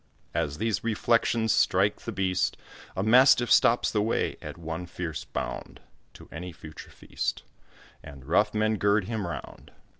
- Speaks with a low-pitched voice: Yes, low, 100 Hz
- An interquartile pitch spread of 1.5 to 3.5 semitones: No, average, 4.3 semitones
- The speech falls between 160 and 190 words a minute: No, average, 150 wpm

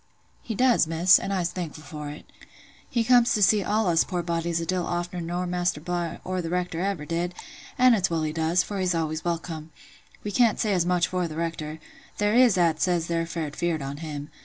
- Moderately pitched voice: Yes, medium, 175 Hz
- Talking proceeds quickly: Yes, fast, 215 wpm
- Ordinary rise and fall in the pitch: No, narrow, 2.2 semitones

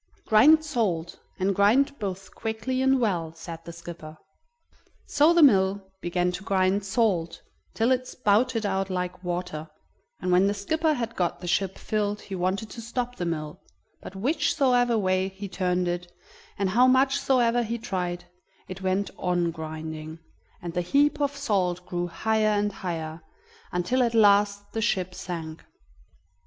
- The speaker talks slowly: No, average, 160 wpm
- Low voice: No, high, 195 Hz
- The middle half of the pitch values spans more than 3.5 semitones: Yes, average, 4.7 semitones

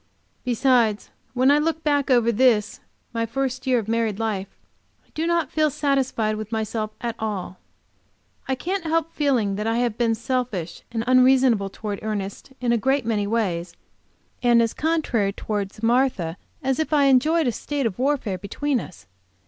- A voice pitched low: No, high, 240 Hz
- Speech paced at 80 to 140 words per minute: No, average, 170 wpm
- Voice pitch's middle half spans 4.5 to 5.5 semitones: No, average, 4.1 semitones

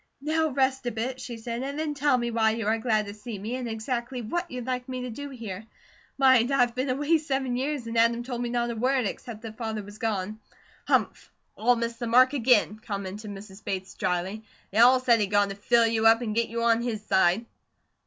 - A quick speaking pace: Yes, fast, 230 wpm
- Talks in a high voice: Yes, high, 235 Hz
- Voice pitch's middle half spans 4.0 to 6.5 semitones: No, average, 2.8 semitones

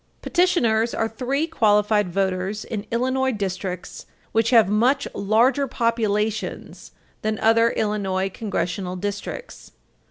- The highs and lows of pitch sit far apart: No, average, 2.8 semitones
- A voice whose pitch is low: No, high, 215 Hz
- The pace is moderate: No, slow, 105 wpm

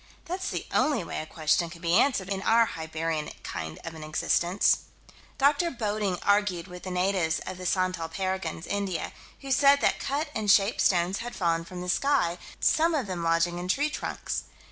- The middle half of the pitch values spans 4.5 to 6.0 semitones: Yes, average, 5.1 semitones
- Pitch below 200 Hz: Yes, medium, 185 Hz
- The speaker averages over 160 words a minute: Yes, average, 190 wpm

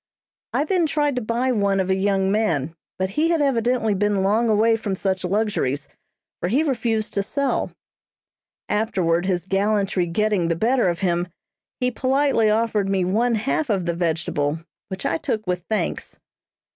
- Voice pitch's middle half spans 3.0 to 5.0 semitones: Yes, average, 3.8 semitones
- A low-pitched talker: No, high, 205 Hz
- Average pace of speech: Yes, average, 170 wpm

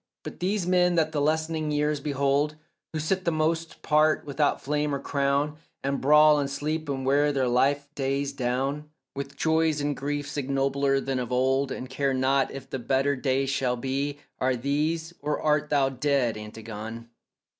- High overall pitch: No, medium, 140 Hz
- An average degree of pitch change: No, narrow, 2.1 semitones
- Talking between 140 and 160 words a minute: No, average, 175 wpm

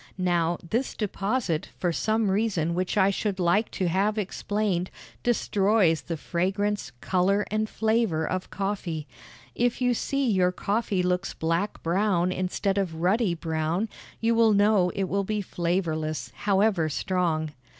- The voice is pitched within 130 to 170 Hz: No, high, 190 Hz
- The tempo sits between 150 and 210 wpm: No, average, 140 wpm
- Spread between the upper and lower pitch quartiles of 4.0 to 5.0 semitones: No, average, 3.5 semitones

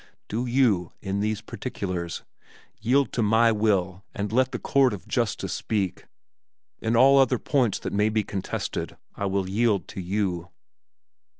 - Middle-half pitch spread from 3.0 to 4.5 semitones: Yes, average, 3.7 semitones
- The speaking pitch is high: No, low, 105 Hz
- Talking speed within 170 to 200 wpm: No, average, 155 wpm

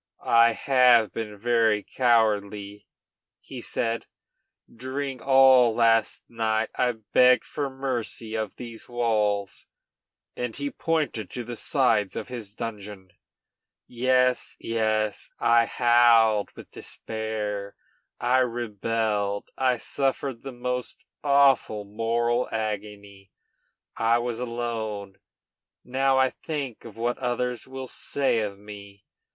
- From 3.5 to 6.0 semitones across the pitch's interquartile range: No, average, 2.9 semitones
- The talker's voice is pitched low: Yes, low, 115 Hz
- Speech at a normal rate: No, slow, 110 wpm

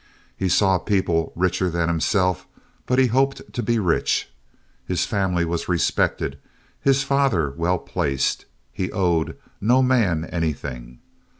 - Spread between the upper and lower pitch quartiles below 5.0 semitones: No, average, 5.3 semitones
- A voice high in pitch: No, very low, 90 Hz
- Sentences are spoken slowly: Yes, slow, 130 wpm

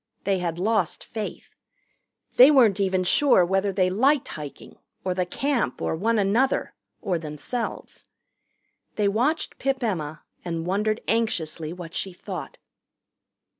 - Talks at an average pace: No, slow, 130 wpm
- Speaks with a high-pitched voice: Yes, high, 195 Hz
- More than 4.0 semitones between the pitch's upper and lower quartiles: Yes, average, 4.5 semitones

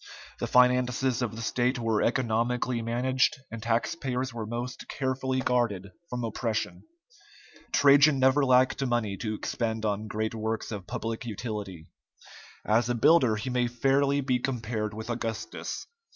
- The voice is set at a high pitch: No, low, 120 Hz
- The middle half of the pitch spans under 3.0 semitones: Yes, narrow, 2.6 semitones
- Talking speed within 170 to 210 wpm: No, average, 140 wpm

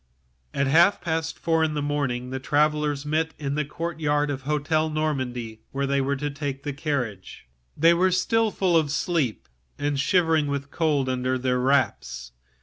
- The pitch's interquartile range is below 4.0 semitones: Yes, average, 2.9 semitones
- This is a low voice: No, medium, 145 Hz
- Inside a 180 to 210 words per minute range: Yes, average, 190 wpm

